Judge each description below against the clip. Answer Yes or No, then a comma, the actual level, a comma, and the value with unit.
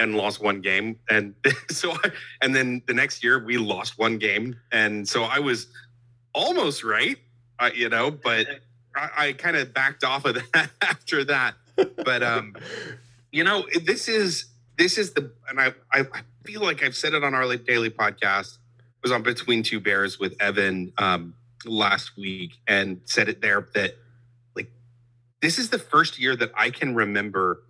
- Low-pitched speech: Yes, low, 120 Hz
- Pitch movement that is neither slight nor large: Yes, average, 3.4 semitones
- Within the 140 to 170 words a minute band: No, average, 180 wpm